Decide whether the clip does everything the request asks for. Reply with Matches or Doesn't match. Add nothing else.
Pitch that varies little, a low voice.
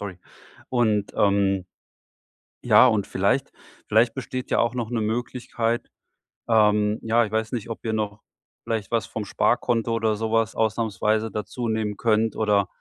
Matches